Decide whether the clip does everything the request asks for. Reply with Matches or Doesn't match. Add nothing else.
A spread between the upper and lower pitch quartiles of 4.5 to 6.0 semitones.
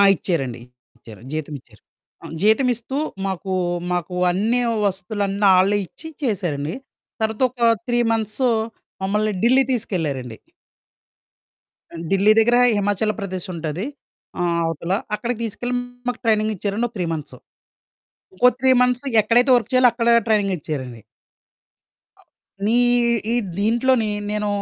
Matches